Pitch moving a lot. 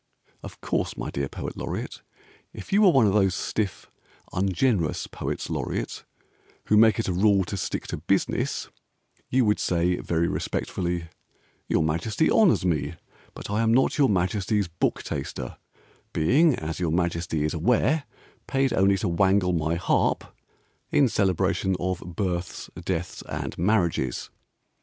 No: average, 4.2 semitones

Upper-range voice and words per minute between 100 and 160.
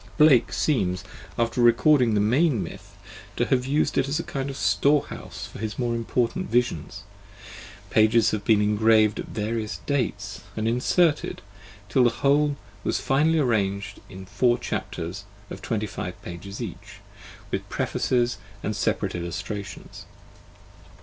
No: low, 115 Hz; average, 140 wpm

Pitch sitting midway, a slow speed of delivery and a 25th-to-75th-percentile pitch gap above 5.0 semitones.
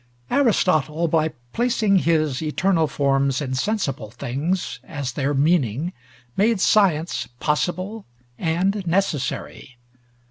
Yes: medium, 160 Hz; slow, 100 wpm; wide, 5.5 semitones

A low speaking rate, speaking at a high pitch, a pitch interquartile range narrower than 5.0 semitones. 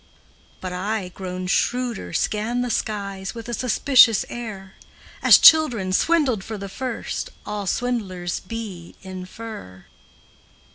Yes: slow, 115 wpm; high, 210 Hz; average, 4.2 semitones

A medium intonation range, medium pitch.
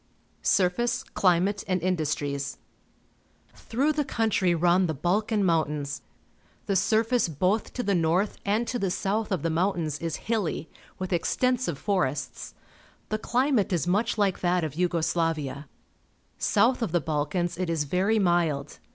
Yes: average, 4.6 semitones; medium, 180 Hz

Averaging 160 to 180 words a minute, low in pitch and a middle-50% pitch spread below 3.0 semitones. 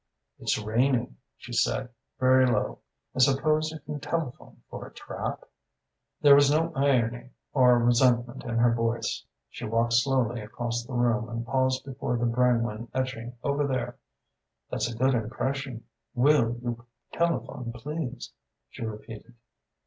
No: average, 140 wpm; low, 125 Hz; narrow, 2.4 semitones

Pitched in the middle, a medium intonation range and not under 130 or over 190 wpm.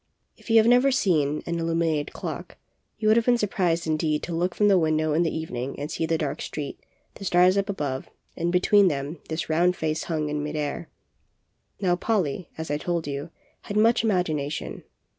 No: medium, 165 Hz; average, 3.7 semitones; average, 200 wpm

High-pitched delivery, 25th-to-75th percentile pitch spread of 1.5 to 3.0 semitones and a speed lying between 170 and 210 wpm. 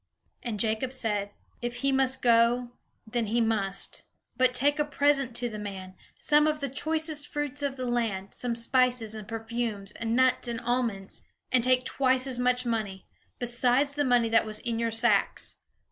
Yes: high, 240 Hz; narrow, 2.5 semitones; average, 175 wpm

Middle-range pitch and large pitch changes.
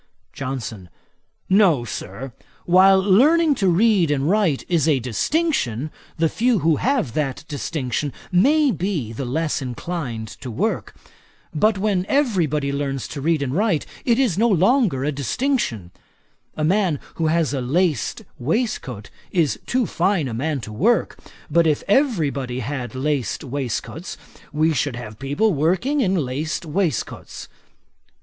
Yes: medium, 155 Hz; wide, 6.7 semitones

